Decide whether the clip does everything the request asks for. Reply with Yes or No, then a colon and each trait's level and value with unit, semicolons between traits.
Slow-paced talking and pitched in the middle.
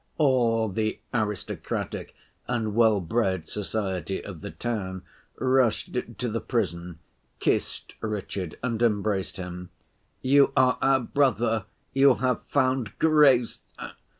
No: slow, 110 wpm; low, 115 Hz